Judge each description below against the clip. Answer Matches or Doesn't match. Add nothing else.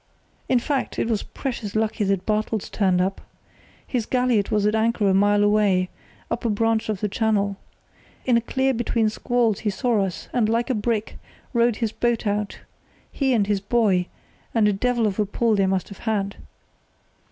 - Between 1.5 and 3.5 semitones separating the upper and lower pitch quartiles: Matches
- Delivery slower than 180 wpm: Doesn't match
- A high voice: Matches